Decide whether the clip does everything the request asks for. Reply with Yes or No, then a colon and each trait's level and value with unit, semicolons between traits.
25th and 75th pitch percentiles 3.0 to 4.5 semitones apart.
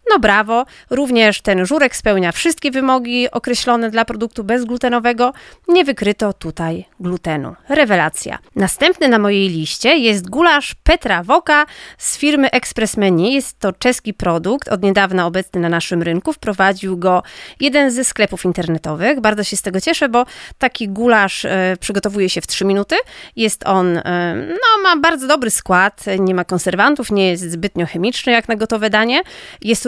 No: wide, 5.5 semitones